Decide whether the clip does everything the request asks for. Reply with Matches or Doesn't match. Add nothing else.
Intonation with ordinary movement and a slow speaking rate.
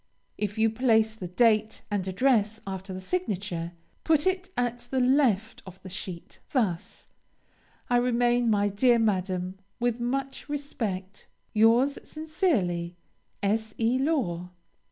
Matches